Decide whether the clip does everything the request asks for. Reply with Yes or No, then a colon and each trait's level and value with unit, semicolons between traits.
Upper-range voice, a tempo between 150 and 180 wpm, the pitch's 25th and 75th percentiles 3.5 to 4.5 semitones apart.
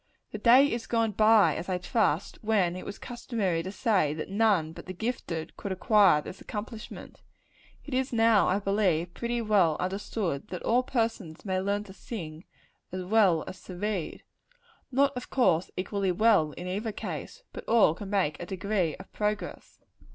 Yes: high, 200 Hz; average, 175 wpm; average, 3.8 semitones